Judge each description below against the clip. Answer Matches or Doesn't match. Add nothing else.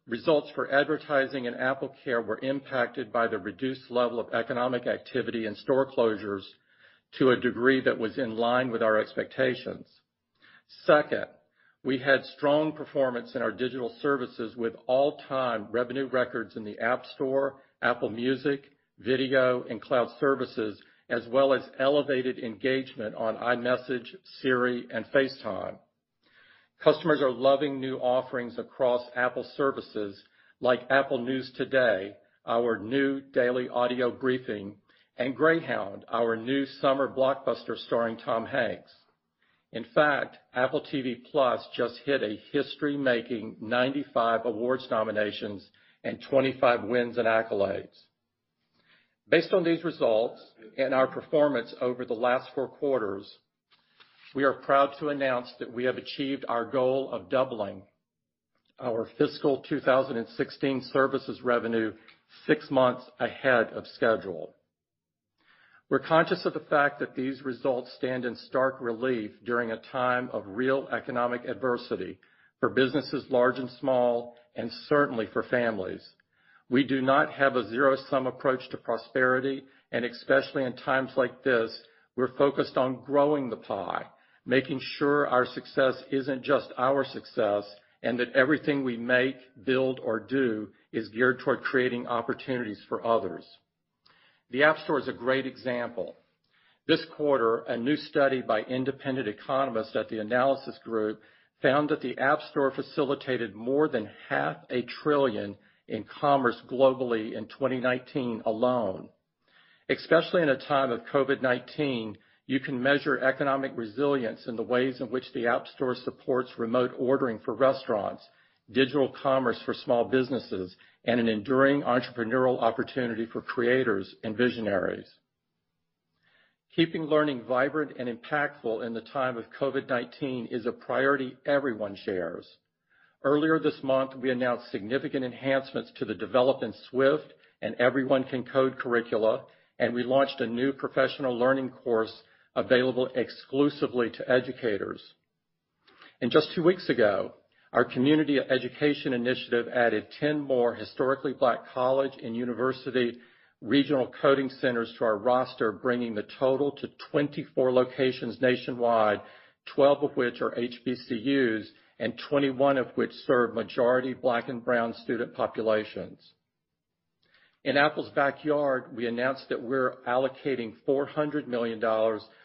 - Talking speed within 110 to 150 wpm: Matches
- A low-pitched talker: Matches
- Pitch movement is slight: Matches